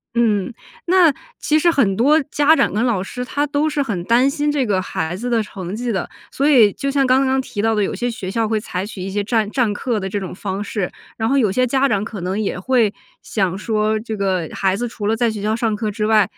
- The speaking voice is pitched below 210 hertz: No, high, 220 Hz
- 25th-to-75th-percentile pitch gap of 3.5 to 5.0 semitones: Yes, average, 4.3 semitones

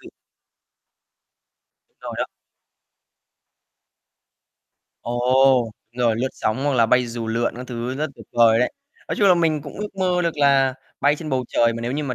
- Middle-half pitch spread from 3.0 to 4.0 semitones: Yes, average, 3.7 semitones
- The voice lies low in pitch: Yes, low, 130 Hz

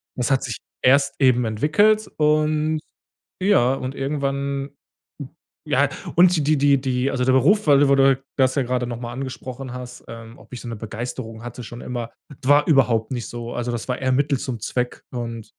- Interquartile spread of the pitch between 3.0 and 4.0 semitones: No, narrow, 2.6 semitones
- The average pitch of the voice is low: Yes, low, 130 Hz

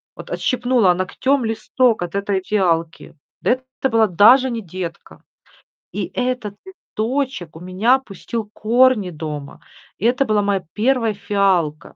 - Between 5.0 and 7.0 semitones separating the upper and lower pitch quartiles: Yes, average, 5.3 semitones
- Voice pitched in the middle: No, high, 215 Hz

